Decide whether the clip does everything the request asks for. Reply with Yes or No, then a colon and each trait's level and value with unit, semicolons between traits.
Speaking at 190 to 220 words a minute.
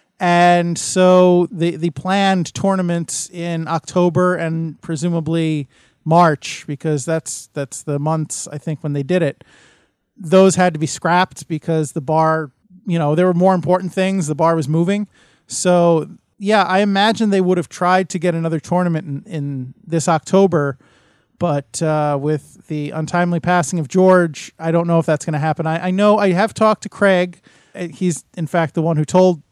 No: average, 180 wpm